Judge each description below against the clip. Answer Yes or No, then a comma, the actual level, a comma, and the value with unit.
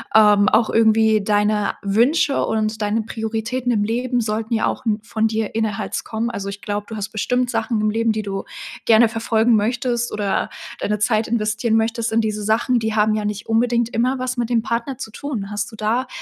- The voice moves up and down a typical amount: No, narrow, 1.8 semitones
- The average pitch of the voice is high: Yes, high, 220 Hz